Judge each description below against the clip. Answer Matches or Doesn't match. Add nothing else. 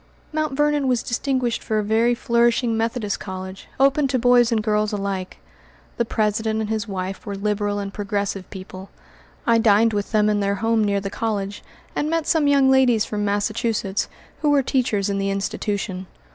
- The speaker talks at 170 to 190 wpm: Matches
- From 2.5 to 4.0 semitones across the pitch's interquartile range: Matches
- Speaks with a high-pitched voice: Matches